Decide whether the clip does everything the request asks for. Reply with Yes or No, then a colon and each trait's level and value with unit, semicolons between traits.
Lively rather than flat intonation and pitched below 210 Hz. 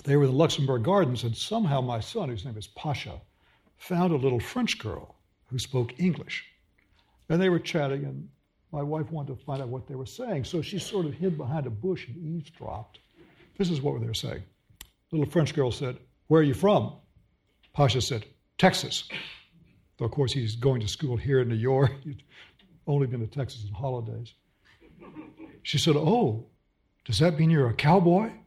Yes: wide, 5.9 semitones; medium, 140 Hz